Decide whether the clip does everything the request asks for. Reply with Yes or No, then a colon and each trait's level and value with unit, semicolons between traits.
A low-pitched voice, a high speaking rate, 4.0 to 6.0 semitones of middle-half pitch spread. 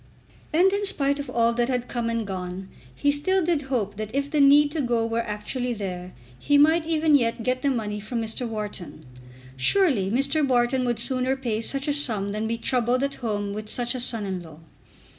No: high, 240 Hz; fast, 210 wpm; average, 4.7 semitones